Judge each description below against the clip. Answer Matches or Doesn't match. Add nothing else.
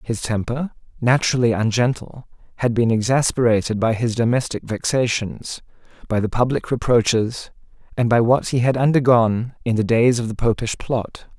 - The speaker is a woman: Doesn't match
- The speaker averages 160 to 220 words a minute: Doesn't match